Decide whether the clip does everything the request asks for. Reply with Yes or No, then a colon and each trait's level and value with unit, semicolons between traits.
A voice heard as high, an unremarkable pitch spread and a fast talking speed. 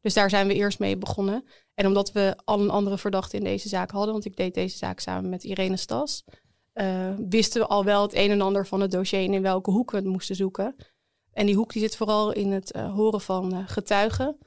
No: high, 200 Hz; narrow, 1.6 semitones; fast, 250 wpm